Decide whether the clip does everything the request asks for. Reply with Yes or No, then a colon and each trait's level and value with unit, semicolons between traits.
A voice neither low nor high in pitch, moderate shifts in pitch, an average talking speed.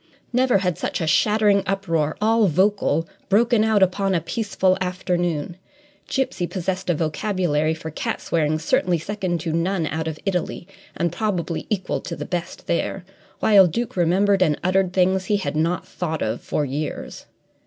Yes: medium, 180 Hz; average, 3.4 semitones; average, 165 wpm